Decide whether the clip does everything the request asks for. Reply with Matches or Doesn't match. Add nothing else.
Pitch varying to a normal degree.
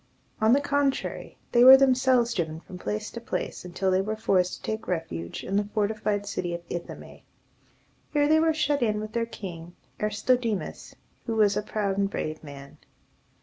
Matches